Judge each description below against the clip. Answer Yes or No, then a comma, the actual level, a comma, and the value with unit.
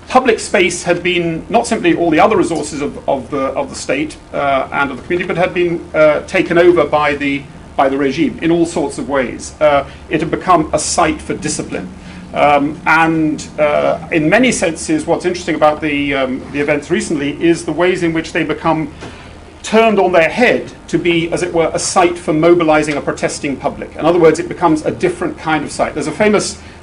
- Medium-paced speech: No, fast, 210 wpm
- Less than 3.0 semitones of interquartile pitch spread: Yes, narrow, 2.6 semitones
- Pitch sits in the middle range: Yes, medium, 165 Hz